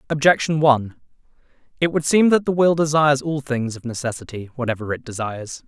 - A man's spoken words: Yes, male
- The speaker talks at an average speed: Yes, average, 170 wpm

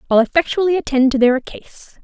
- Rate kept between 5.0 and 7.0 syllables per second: Yes, 5.7 syllables/s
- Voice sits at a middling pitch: No, very high, 280 Hz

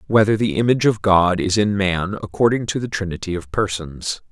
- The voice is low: Yes, low, 100 Hz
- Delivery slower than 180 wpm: No, average, 195 wpm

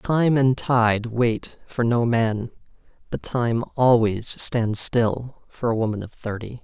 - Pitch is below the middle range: Yes, low, 115 Hz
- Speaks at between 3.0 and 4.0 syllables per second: Yes, 3.4 syllables/s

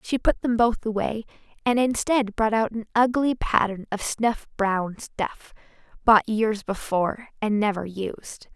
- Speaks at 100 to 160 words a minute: Yes, average, 155 wpm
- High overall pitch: Yes, high, 220 Hz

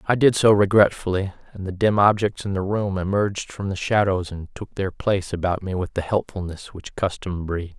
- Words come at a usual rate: No, fast, 210 wpm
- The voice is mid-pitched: No, very low, 95 Hz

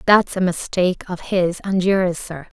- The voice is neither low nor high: Yes, medium, 180 Hz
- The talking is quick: No, average, 185 wpm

